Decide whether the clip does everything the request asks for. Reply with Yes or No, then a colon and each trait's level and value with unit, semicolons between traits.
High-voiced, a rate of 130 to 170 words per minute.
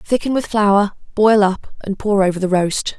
No: high, 205 Hz; average, 200 wpm